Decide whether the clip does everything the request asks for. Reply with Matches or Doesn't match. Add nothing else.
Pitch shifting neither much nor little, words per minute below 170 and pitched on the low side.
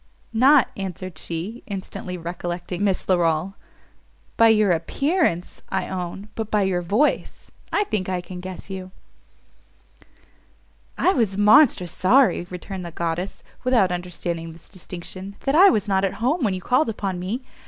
Doesn't match